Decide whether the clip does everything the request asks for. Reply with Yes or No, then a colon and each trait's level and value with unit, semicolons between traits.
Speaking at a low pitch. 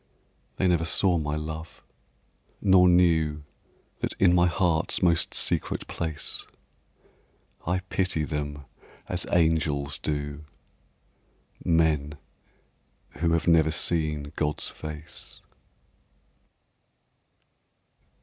Yes: very low, 80 Hz